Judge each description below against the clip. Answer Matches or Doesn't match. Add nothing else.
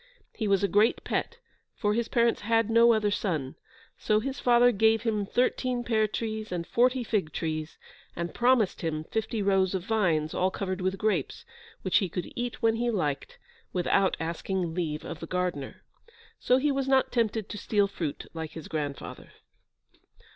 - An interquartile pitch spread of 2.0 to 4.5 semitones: Doesn't match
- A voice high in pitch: Matches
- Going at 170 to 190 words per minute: Matches